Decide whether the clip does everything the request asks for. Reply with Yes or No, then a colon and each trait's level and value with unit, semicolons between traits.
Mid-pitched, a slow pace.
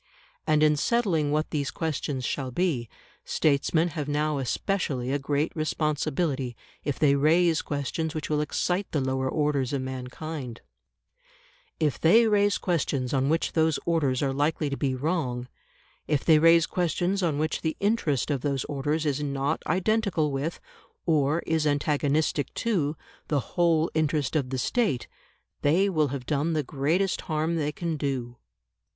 No: medium, 150 Hz; average, 155 wpm